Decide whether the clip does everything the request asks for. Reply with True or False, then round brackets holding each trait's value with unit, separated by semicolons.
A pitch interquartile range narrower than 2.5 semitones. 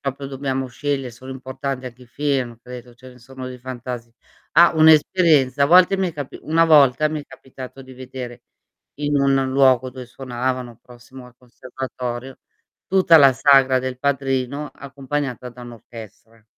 True (2.0 semitones)